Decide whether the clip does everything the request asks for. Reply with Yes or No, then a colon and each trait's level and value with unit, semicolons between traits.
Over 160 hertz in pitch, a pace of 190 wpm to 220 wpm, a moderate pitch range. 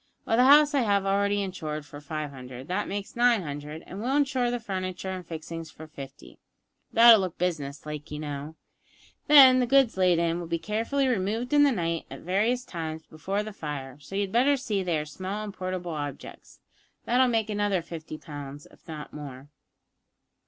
No: medium, 185 Hz; average, 195 wpm; wide, 6.5 semitones